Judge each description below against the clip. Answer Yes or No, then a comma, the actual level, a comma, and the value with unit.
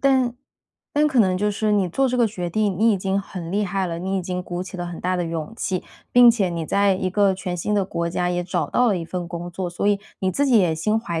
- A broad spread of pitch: No, average, 3.1 semitones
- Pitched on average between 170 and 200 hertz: Yes, high, 190 Hz